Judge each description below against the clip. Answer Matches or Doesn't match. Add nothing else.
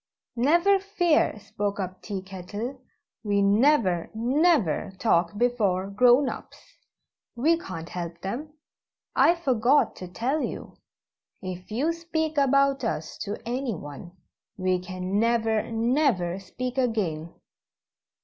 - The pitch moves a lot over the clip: Matches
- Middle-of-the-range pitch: Doesn't match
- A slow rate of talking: Matches